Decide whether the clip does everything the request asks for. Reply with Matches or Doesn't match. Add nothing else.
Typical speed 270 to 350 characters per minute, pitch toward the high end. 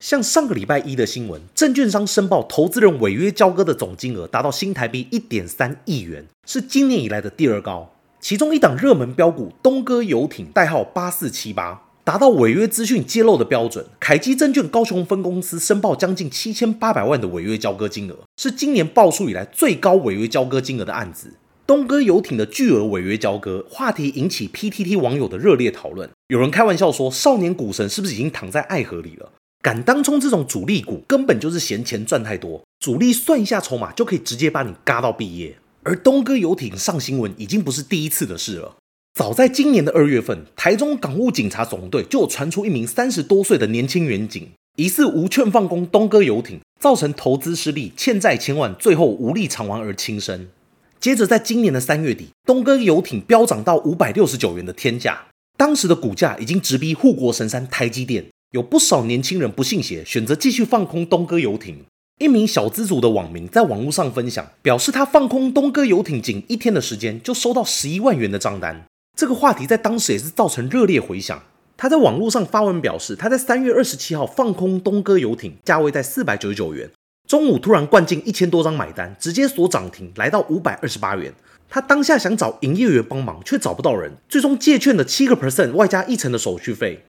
Matches